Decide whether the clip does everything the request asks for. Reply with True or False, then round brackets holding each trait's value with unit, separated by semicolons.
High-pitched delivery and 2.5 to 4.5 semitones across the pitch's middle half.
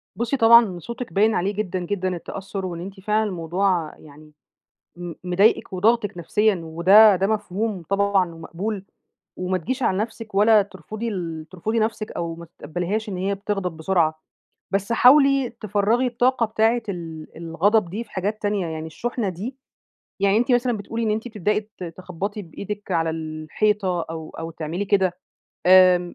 True (195 Hz; 3.9 semitones)